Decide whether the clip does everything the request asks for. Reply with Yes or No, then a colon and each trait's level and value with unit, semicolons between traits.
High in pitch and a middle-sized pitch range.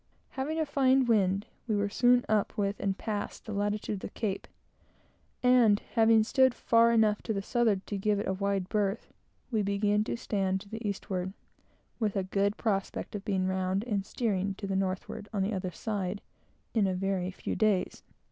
No: high, 205 Hz; narrow, 2.3 semitones